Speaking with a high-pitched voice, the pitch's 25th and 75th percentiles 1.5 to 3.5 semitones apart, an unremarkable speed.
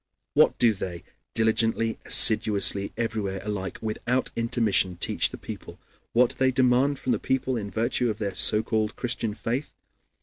No: low, 115 Hz; average, 2.9 semitones; average, 160 wpm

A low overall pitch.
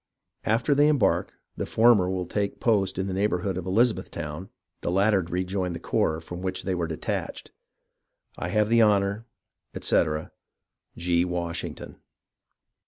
Yes: very low, 95 Hz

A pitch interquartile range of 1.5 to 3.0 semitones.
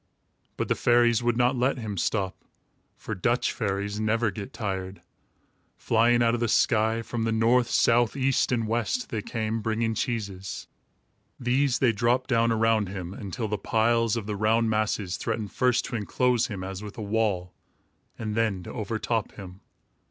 Yes: narrow, 2.4 semitones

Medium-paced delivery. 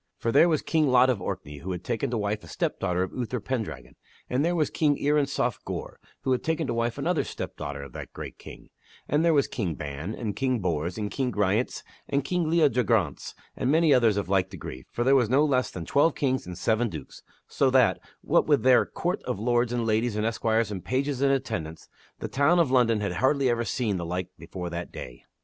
No: fast, 225 wpm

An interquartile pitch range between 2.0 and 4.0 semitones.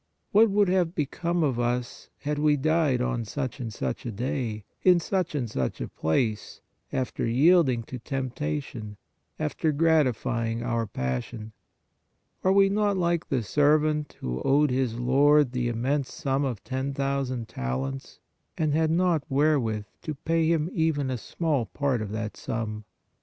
No: average, 4.9 semitones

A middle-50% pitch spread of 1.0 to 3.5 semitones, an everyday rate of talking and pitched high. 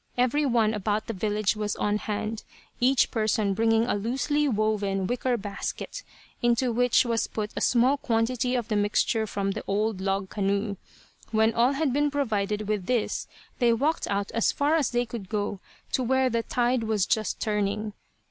Yes: average, 3.1 semitones; average, 175 wpm; high, 220 Hz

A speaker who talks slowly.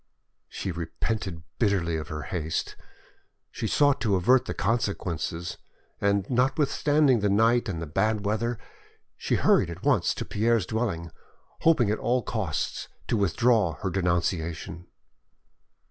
Yes: slow, 130 wpm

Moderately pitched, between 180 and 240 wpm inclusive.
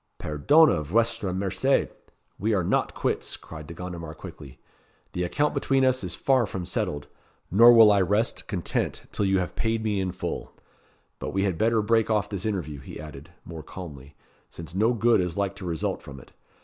No: very low, 95 Hz; average, 190 wpm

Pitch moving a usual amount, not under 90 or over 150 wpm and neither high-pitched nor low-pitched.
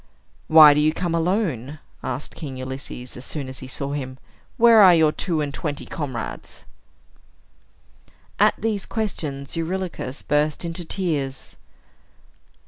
Yes: average, 4.3 semitones; slow, 135 wpm; medium, 150 Hz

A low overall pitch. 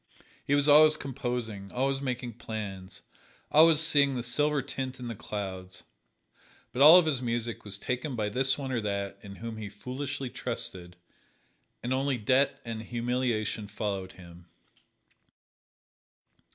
Yes: low, 120 Hz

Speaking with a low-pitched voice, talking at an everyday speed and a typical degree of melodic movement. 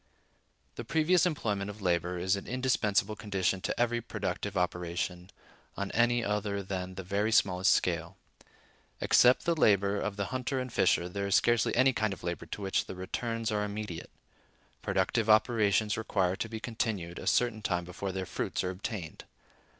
Yes: low, 100 Hz; average, 170 wpm; average, 3.4 semitones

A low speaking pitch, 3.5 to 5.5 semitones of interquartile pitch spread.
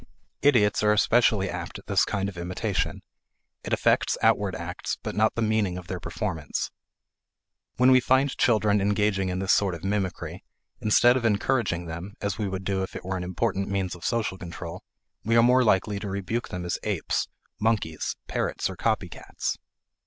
No: low, 100 Hz; average, 3.1 semitones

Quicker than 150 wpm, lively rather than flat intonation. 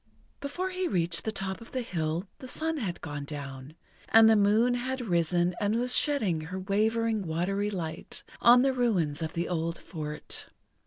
Yes: average, 175 wpm; wide, 6.2 semitones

